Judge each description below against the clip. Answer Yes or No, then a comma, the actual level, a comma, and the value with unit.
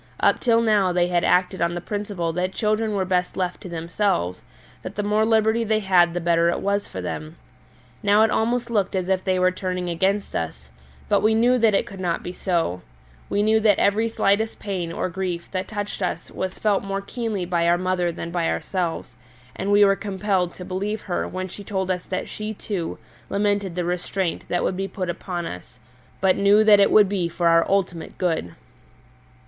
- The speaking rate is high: Yes, fast, 210 wpm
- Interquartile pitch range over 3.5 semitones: No, average, 2.7 semitones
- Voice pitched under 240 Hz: Yes, high, 190 Hz